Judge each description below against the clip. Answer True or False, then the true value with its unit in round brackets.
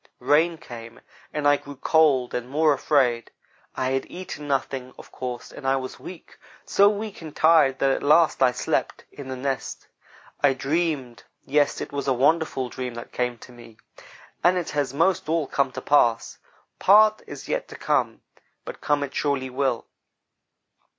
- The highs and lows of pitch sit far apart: False (3.6 semitones)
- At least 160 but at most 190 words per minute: True (175 wpm)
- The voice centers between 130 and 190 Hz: True (140 Hz)